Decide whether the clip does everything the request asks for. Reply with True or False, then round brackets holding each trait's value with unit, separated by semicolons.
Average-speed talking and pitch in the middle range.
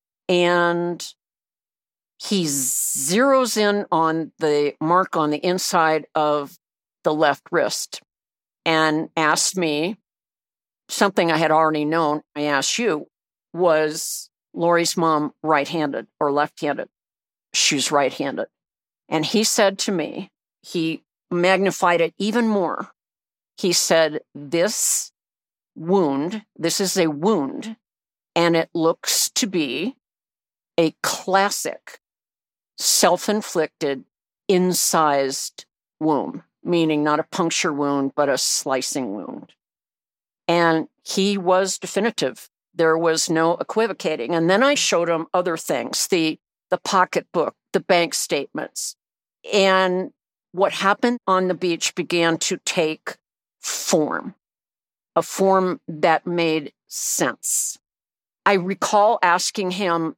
False (115 wpm; 170 Hz)